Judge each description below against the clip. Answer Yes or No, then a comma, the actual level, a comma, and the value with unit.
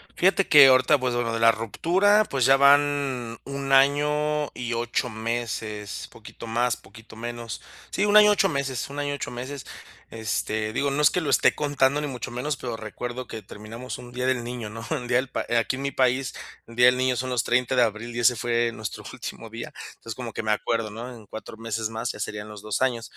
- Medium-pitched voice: No, low, 125 Hz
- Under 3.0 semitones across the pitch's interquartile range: No, average, 3.3 semitones